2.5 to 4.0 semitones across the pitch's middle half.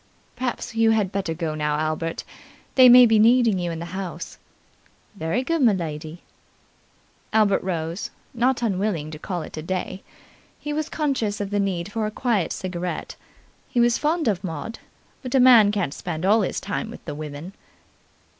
No: wide, 5.6 semitones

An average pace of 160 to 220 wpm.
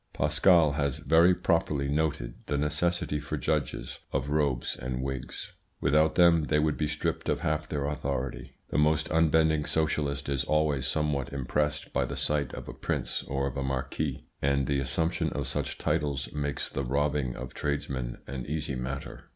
Yes: average, 165 wpm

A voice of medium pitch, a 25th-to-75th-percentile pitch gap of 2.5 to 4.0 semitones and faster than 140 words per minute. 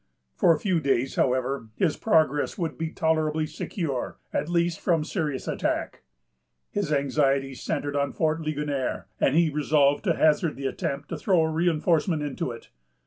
Yes: medium, 155 Hz; average, 2.8 semitones; average, 160 wpm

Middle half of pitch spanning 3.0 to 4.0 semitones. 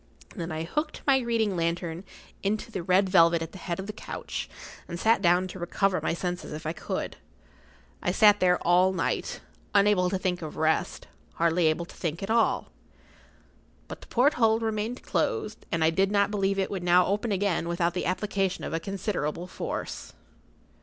Yes: average, 3.3 semitones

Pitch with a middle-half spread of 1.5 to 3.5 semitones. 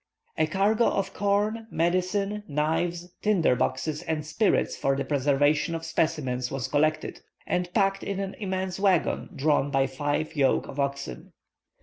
No: average, 5.1 semitones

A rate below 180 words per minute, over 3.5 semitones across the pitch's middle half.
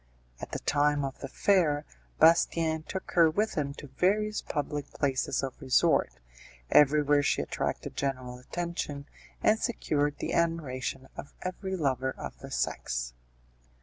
Yes: average, 140 wpm; average, 3.9 semitones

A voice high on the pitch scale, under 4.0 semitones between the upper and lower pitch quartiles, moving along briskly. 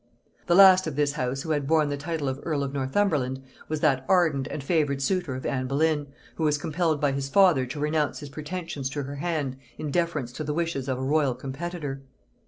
No: medium, 145 Hz; average, 3.0 semitones; fast, 215 wpm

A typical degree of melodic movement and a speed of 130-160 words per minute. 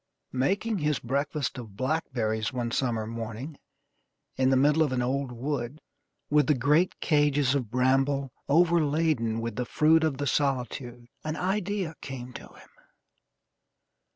Yes: average, 3.7 semitones; average, 140 wpm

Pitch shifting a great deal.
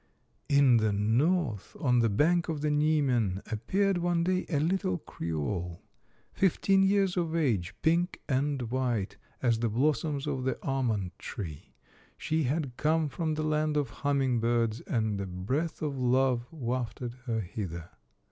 Yes: wide, 5.8 semitones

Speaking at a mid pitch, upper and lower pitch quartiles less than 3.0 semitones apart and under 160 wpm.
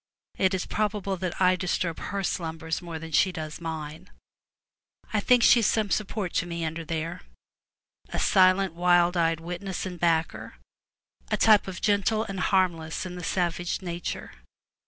No: medium, 180 Hz; narrow, 2.6 semitones; average, 165 wpm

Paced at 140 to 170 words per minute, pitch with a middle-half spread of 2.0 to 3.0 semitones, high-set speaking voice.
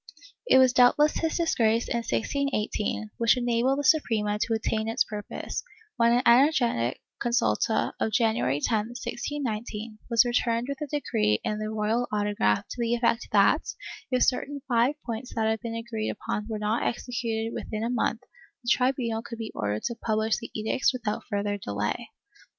Yes: average, 165 wpm; narrow, 2.5 semitones; high, 230 Hz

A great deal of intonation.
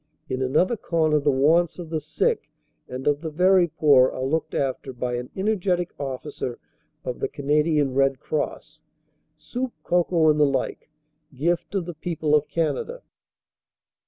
No: average, 4.0 semitones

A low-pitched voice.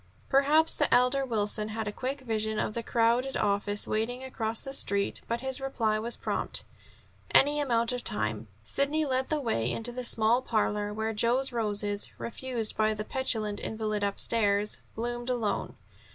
No: high, 230 Hz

